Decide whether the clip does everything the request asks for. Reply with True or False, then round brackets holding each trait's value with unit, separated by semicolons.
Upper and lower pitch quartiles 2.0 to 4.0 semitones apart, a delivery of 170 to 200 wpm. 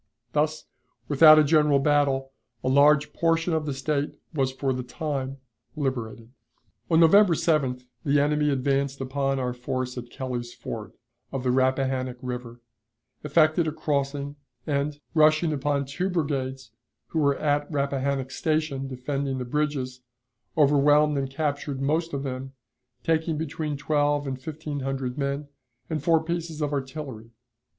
False (2.4 semitones; 145 wpm)